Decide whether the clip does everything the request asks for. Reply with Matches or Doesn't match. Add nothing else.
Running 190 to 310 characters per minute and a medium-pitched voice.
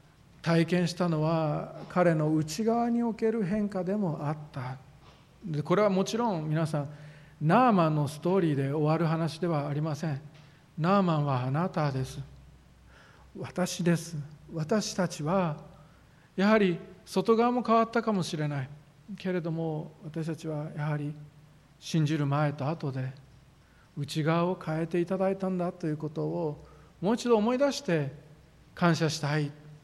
Matches